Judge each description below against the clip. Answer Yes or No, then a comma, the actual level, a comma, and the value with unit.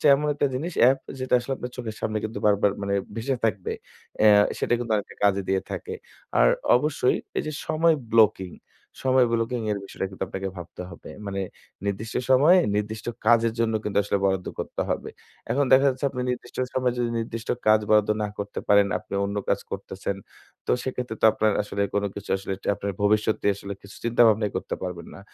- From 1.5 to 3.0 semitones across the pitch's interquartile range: No, average, 3.8 semitones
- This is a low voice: Yes, low, 110 Hz